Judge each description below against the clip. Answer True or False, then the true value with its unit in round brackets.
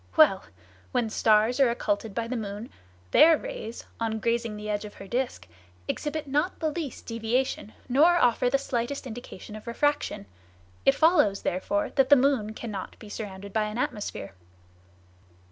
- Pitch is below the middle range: False (235 Hz)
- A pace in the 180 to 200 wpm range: False (160 wpm)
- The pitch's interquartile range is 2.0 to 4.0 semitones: False (4.5 semitones)